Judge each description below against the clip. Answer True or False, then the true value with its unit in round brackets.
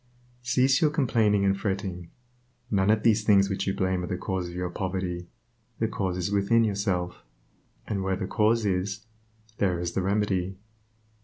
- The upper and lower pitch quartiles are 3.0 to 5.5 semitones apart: False (2.5 semitones)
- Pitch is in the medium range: False (95 Hz)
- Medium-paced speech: True (170 wpm)